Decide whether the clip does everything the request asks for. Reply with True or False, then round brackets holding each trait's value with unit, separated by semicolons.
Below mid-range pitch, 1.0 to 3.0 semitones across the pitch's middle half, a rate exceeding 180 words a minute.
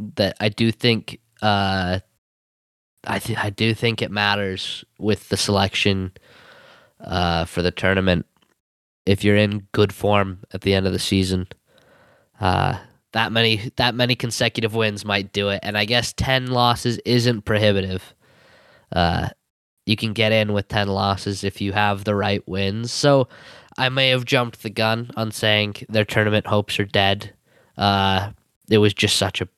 False (105 Hz; 2.5 semitones; 165 wpm)